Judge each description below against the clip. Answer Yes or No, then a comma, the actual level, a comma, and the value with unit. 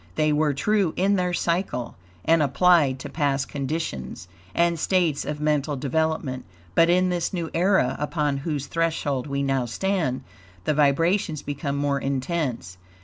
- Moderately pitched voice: Yes, medium, 150 Hz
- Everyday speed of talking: Yes, average, 145 wpm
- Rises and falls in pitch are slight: No, average, 3.6 semitones